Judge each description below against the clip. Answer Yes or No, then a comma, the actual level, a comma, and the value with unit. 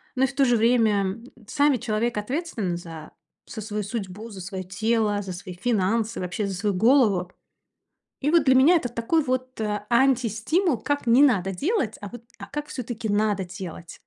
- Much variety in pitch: No, average, 4.5 semitones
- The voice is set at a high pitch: Yes, high, 220 Hz